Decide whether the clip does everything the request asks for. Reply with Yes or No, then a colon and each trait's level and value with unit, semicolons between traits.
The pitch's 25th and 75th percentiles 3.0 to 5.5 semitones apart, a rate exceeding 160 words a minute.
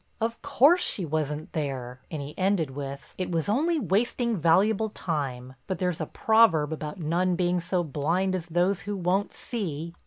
Yes: average, 4.8 semitones; average, 175 wpm